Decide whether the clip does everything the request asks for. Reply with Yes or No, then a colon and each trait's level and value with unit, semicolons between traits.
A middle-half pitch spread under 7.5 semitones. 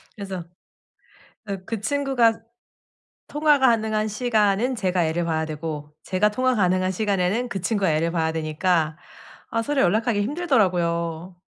Yes: average, 5.3 semitones